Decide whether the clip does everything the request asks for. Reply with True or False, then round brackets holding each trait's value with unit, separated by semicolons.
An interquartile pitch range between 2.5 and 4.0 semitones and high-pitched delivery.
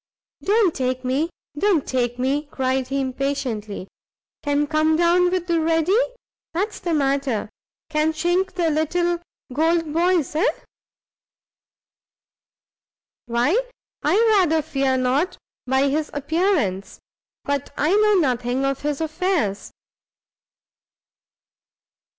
False (4.5 semitones; 300 Hz)